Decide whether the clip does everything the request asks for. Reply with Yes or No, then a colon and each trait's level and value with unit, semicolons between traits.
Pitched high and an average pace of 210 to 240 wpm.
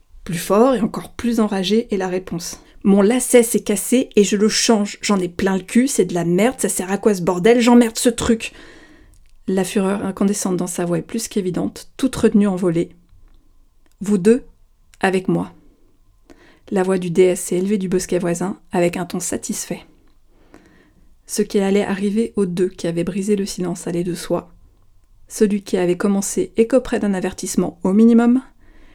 No: high, 195 Hz; average, 180 wpm